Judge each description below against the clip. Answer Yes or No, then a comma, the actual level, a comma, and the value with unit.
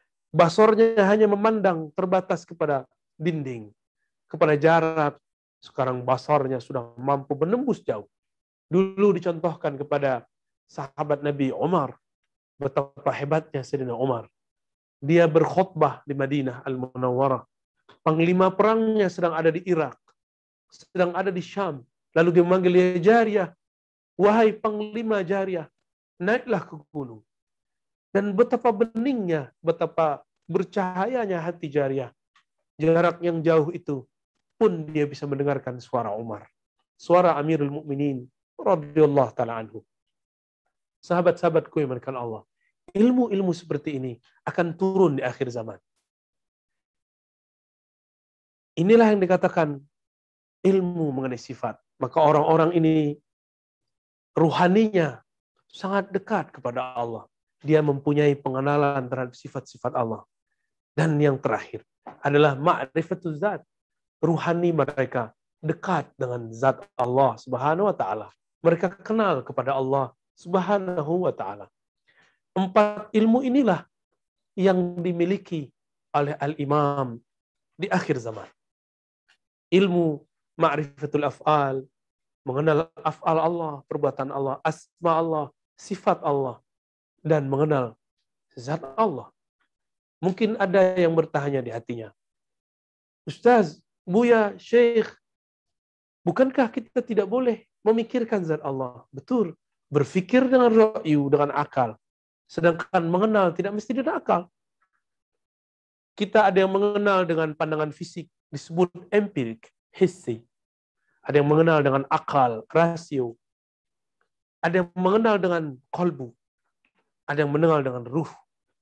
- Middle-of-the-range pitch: Yes, medium, 155 Hz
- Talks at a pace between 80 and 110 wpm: Yes, average, 105 wpm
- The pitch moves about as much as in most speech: No, wide, 5.7 semitones